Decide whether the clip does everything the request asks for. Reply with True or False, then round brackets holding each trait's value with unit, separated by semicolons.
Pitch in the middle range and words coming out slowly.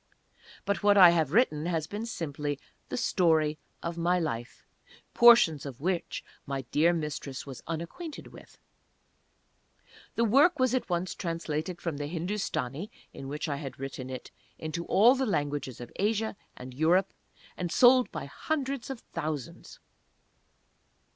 False (170 Hz; 145 wpm)